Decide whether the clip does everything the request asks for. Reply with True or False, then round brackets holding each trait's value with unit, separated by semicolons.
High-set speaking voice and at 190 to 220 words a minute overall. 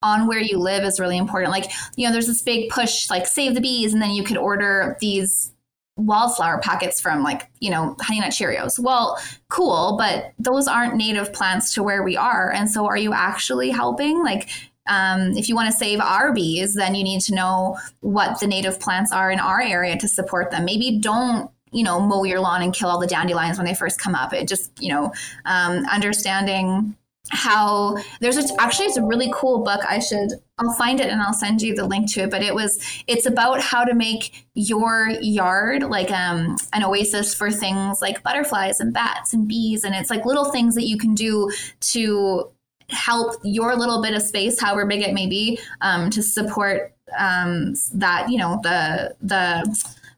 True (210 Hz; 205 wpm)